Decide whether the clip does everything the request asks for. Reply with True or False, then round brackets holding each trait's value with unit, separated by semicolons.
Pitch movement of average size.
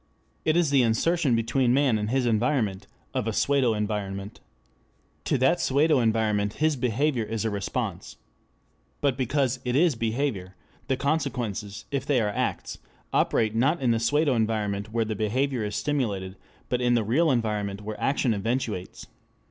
True (4.4 semitones)